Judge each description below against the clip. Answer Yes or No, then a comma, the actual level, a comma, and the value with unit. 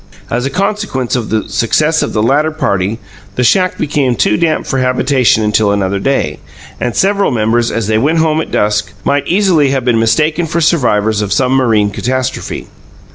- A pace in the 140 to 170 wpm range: No, average, 185 wpm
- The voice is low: Yes, low, 125 Hz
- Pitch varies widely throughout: Yes, wide, 5.9 semitones